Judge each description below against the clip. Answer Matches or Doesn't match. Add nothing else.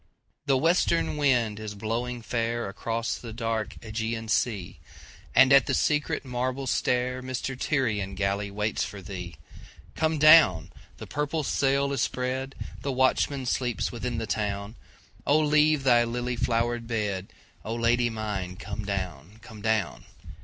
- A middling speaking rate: Doesn't match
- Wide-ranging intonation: Doesn't match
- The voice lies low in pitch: Matches